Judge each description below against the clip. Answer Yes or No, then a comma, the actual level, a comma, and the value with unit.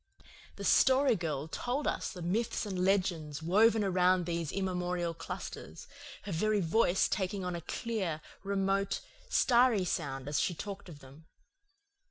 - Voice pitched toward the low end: No, medium, 185 Hz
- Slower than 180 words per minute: Yes, average, 145 wpm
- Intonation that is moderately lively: Yes, average, 3.6 semitones